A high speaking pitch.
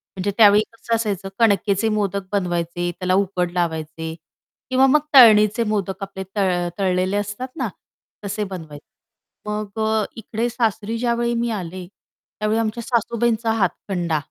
Yes: high, 205 Hz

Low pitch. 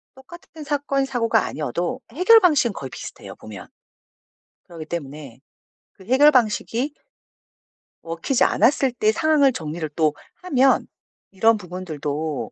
No: high, 225 Hz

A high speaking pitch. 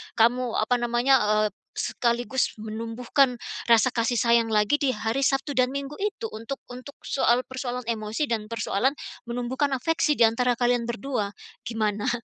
Yes: high, 240 Hz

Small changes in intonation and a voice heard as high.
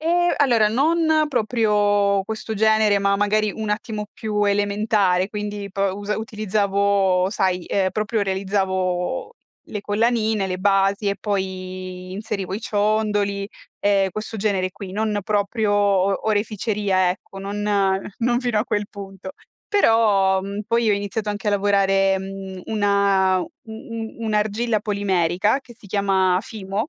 Yes: narrow, 1.9 semitones; high, 205 Hz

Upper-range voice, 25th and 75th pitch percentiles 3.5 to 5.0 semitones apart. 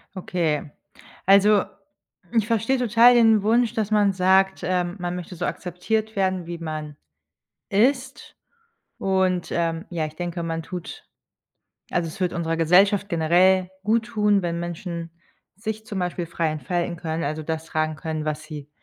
No: medium, 180 Hz; average, 3.8 semitones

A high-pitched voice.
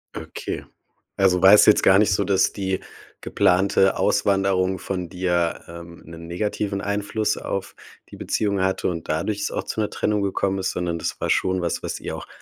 No: very low, 95 Hz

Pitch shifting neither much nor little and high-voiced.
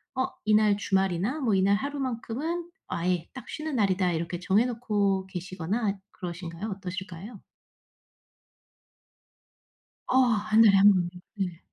Yes: average, 3.8 semitones; high, 200 Hz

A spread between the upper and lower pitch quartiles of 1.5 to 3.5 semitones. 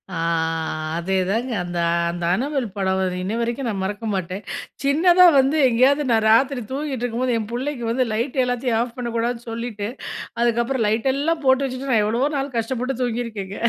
Yes: average, 3.2 semitones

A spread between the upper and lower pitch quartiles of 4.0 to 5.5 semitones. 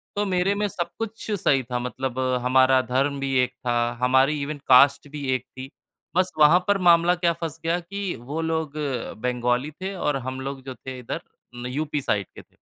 Yes: average, 4.8 semitones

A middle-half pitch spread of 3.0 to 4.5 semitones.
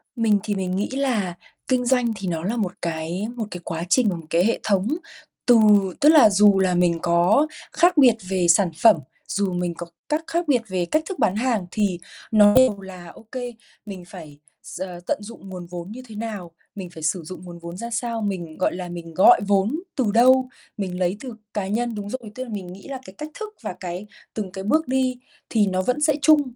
No: average, 5.2 semitones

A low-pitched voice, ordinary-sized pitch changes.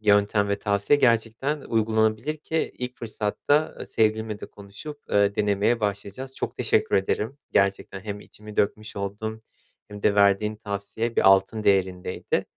No: low, 105 Hz; narrow, 2.0 semitones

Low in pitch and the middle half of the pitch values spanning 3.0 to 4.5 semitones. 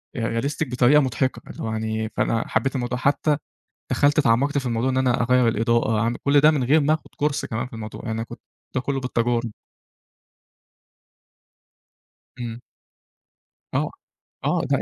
Yes: low, 125 Hz; average, 3.4 semitones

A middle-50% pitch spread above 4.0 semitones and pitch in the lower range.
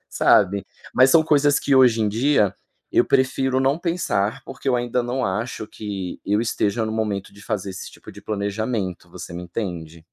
Yes: average, 4.7 semitones; low, 110 Hz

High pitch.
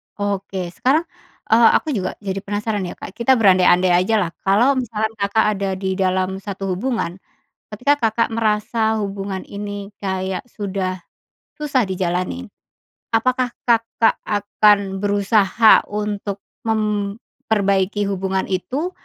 Yes: high, 205 Hz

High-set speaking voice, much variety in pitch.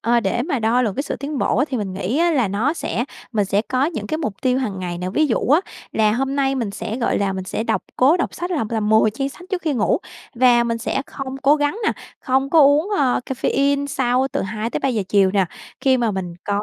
No: very high, 250 Hz; average, 4.6 semitones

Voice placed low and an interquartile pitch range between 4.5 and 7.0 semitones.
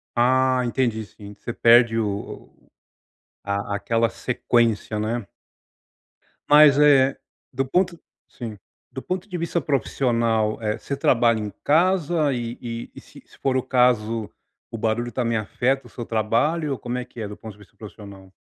No: low, 120 Hz; average, 3.5 semitones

